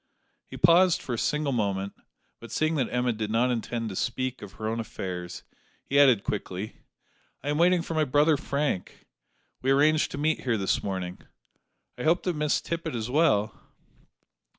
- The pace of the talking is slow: No, average, 175 wpm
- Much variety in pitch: Yes, wide, 5.9 semitones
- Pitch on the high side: No, low, 125 Hz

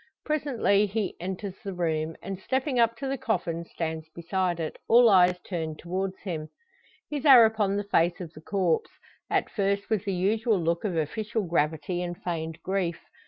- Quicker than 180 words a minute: No, average, 175 wpm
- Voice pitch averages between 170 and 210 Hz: Yes, medium, 185 Hz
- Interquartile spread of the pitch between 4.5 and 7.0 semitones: No, average, 4.1 semitones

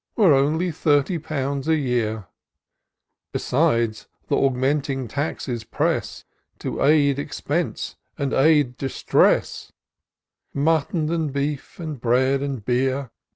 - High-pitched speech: No, medium, 140 Hz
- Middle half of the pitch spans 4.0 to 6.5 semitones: No, average, 2.7 semitones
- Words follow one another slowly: Yes, slow, 110 wpm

